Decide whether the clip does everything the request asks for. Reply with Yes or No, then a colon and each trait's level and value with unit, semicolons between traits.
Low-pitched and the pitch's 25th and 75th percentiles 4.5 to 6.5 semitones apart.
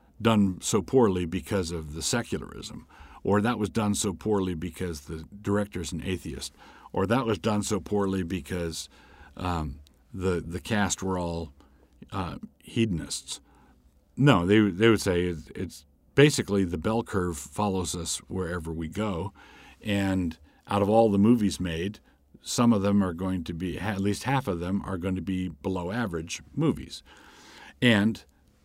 No: very low, 95 Hz; average, 3.5 semitones